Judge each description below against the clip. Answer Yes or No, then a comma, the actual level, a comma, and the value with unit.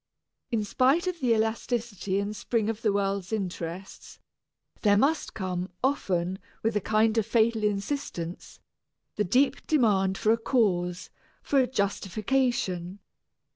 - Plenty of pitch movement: No, average, 3.8 semitones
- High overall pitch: Yes, high, 215 Hz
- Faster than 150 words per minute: No, slow, 135 wpm